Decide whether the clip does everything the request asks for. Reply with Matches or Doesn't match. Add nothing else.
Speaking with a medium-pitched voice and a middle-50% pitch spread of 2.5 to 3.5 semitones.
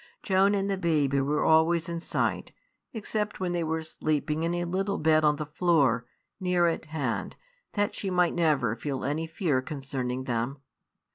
Doesn't match